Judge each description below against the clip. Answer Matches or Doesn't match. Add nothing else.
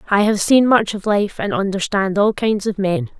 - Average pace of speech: Doesn't match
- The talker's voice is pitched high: Matches